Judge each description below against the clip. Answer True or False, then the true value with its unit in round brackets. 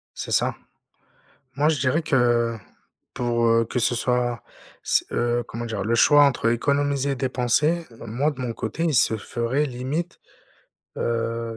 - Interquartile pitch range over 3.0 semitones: True (3.4 semitones)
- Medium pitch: False (120 Hz)